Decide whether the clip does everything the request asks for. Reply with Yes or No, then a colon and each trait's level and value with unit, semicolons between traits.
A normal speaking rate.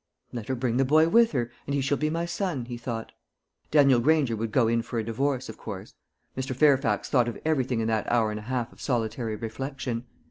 No: fast, 225 wpm